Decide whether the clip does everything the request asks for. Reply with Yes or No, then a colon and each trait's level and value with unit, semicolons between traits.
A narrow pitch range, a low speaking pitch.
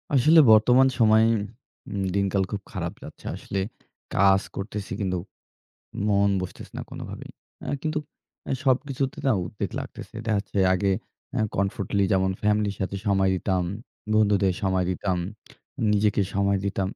Yes: narrow, 1.9 semitones; low, 100 Hz